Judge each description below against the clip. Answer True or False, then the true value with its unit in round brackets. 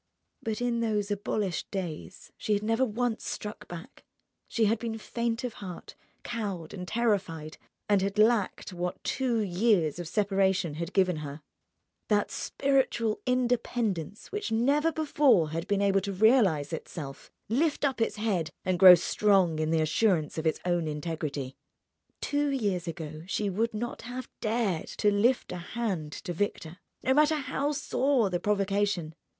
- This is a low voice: False (205 Hz)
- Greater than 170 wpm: False (155 wpm)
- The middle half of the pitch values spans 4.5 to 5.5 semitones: True (5.1 semitones)